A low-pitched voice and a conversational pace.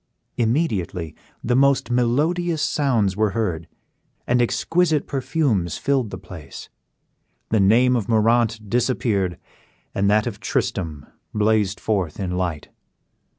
No: low, 110 Hz; slow, 115 wpm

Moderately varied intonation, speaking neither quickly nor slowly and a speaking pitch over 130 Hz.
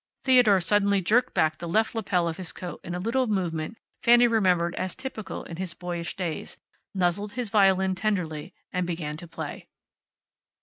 Yes: average, 3.8 semitones; average, 170 wpm; medium, 185 Hz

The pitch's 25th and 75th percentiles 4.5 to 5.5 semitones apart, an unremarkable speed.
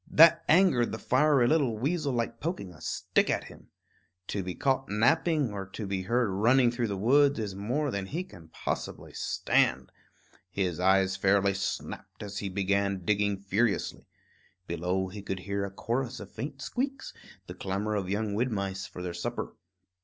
Yes: average, 5.1 semitones; average, 175 wpm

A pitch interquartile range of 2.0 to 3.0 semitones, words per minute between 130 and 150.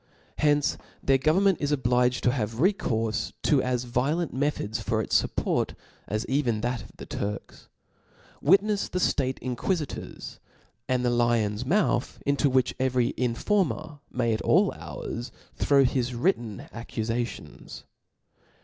No: average, 3.7 semitones; average, 140 wpm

